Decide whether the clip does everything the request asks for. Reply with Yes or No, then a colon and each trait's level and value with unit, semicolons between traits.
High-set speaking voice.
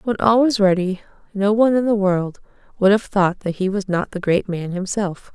Yes: high, 200 Hz